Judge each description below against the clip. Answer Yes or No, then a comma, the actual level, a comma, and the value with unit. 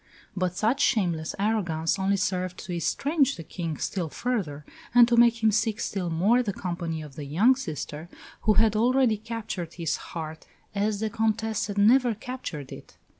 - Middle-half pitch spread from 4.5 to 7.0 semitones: Yes, average, 5.2 semitones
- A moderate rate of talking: Yes, average, 175 wpm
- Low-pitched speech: No, high, 205 Hz